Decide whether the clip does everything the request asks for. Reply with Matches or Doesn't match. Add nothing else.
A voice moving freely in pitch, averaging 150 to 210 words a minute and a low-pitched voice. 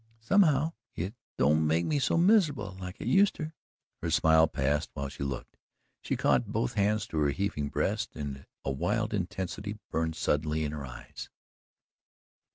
Matches